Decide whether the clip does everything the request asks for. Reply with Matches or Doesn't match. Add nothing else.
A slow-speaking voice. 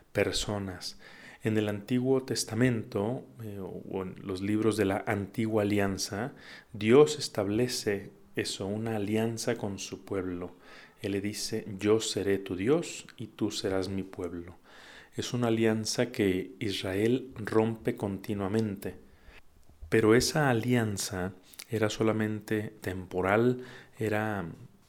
Matches